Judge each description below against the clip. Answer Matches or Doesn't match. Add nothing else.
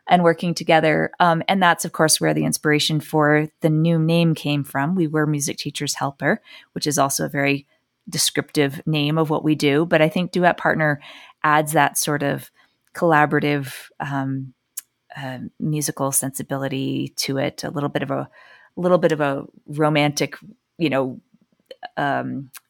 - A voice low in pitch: Doesn't match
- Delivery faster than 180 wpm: Doesn't match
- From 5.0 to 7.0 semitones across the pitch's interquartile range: Doesn't match